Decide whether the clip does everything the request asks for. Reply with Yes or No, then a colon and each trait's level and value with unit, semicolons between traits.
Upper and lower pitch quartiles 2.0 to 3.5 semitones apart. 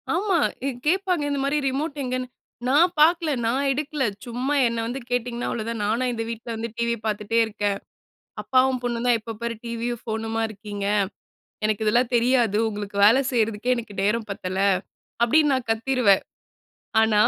Yes: average, 2.9 semitones